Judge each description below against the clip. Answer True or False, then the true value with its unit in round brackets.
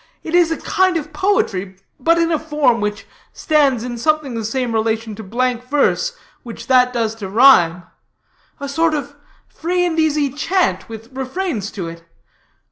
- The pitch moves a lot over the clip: True (5.9 semitones)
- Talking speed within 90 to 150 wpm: False (170 wpm)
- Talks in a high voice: True (265 Hz)